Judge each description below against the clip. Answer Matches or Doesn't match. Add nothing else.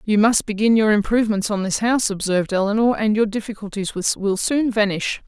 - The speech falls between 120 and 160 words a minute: Doesn't match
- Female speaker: Matches